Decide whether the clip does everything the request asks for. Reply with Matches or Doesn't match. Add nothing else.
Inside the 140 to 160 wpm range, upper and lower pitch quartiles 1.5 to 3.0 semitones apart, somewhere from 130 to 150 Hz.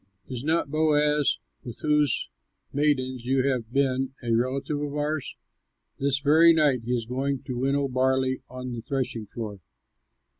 Matches